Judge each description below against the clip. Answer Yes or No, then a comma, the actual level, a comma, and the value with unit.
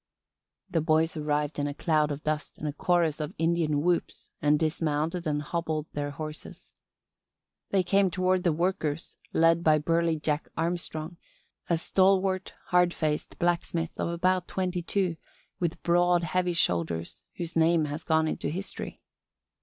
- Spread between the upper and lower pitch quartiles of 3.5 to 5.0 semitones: No, narrow, 2.5 semitones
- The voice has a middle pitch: Yes, medium, 165 Hz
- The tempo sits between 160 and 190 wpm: No, average, 150 wpm